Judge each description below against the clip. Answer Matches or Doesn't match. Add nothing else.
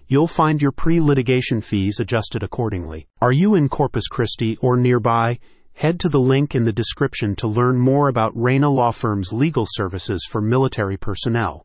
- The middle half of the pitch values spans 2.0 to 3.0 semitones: Doesn't match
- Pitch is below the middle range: Matches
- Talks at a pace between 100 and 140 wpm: Doesn't match